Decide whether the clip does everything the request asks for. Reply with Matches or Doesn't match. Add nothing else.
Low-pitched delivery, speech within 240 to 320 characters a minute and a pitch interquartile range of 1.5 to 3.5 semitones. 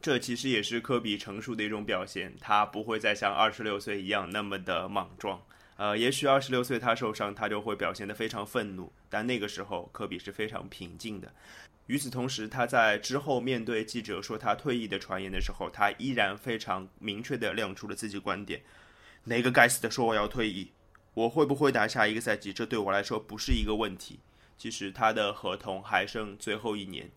Matches